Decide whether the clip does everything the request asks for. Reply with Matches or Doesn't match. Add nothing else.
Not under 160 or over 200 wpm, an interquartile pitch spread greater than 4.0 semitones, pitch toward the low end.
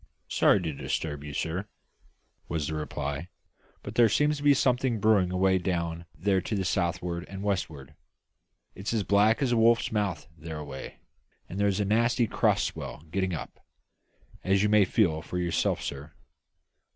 Matches